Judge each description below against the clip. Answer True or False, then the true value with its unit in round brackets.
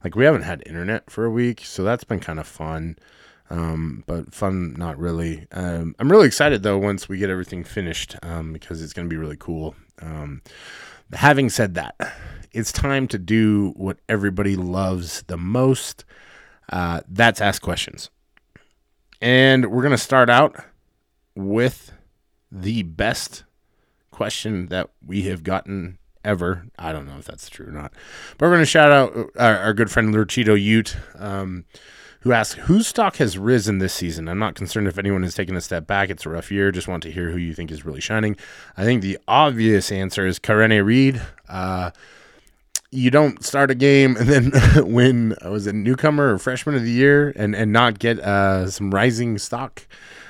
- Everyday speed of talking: True (185 wpm)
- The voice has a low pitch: True (100 Hz)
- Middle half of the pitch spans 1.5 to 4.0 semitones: False (5.1 semitones)